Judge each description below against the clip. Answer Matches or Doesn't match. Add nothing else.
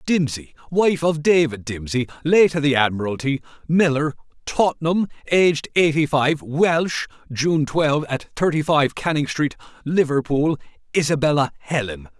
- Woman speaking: Doesn't match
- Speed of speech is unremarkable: Doesn't match